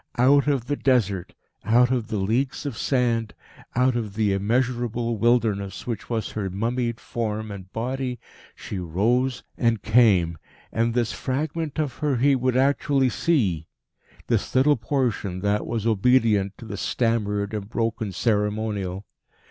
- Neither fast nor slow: Yes, average, 145 wpm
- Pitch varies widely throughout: No, average, 3.6 semitones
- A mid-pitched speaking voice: No, low, 115 Hz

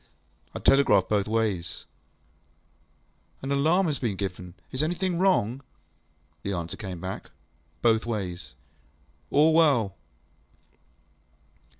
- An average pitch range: No, wide, 7.3 semitones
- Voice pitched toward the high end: No, low, 110 Hz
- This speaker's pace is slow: Yes, slow, 100 wpm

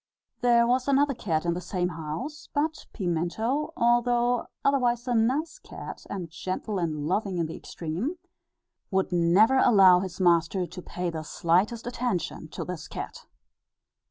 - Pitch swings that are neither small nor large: No, wide, 6.0 semitones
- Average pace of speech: Yes, average, 150 wpm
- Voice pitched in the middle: No, high, 195 Hz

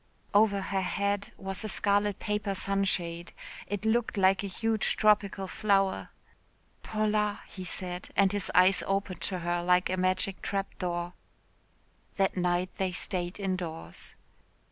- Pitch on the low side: No, high, 195 Hz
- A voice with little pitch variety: Yes, narrow, 1.9 semitones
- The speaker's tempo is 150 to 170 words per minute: No, average, 140 wpm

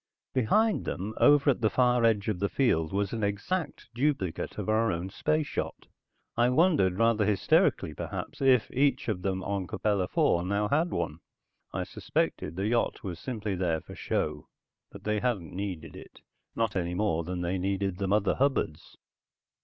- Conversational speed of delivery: Yes, average, 175 wpm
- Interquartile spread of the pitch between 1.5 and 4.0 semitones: No, average, 5.0 semitones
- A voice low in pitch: Yes, low, 105 Hz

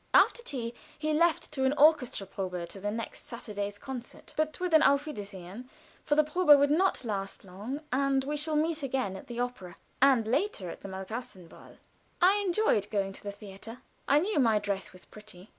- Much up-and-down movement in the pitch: Yes, wide, 6.9 semitones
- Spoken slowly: No, average, 195 wpm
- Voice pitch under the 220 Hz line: No, very high, 250 Hz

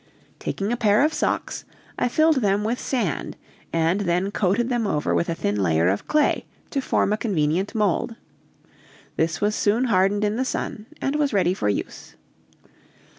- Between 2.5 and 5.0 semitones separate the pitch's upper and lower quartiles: No, wide, 5.6 semitones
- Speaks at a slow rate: No, average, 175 wpm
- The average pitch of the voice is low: No, high, 205 Hz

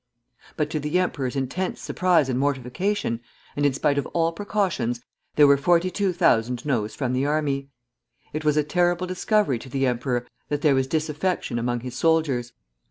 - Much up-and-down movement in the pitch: No, average, 4.7 semitones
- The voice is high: No, medium, 145 Hz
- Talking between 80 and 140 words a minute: No, average, 165 wpm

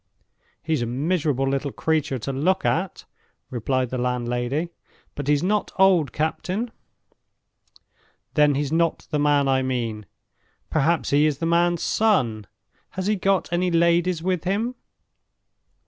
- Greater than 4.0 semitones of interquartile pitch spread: Yes, average, 5.0 semitones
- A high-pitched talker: No, medium, 155 Hz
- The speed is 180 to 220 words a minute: No, slow, 135 wpm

